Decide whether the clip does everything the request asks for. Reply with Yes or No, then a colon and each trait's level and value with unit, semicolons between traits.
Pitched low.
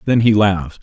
Yes: low, 100 Hz